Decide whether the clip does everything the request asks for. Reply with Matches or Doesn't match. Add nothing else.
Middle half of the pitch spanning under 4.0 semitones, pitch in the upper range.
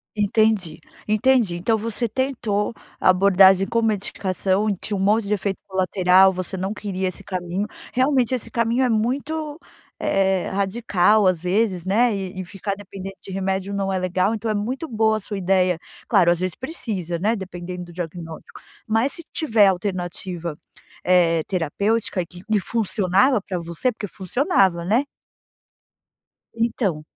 Matches